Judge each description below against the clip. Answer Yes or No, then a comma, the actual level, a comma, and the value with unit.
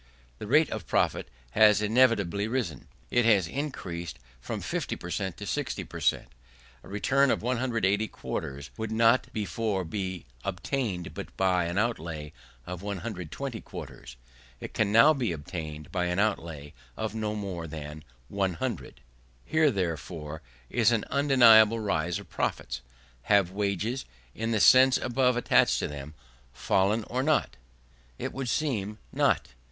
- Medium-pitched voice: No, low, 105 Hz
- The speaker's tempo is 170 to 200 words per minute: No, average, 145 wpm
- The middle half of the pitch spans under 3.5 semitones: No, average, 5.2 semitones